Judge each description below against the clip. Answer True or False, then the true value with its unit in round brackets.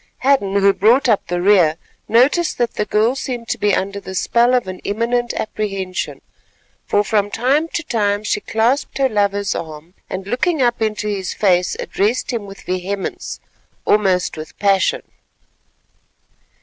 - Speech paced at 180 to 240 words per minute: False (155 wpm)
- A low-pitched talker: False (210 Hz)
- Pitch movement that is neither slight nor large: True (3.7 semitones)